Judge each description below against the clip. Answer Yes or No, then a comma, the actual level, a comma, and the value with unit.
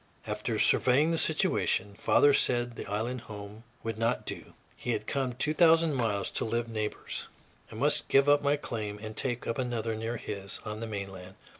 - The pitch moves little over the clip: No, average, 3.6 semitones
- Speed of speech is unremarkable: Yes, average, 185 wpm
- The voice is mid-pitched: No, low, 115 Hz